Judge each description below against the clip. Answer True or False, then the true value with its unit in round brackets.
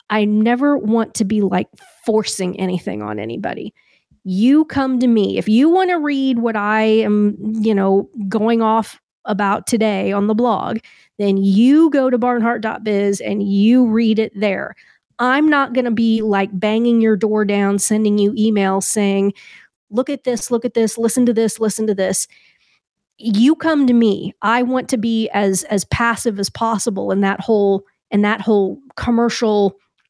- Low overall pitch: False (220 Hz)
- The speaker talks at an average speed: True (175 wpm)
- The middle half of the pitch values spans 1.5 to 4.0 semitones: True (2.8 semitones)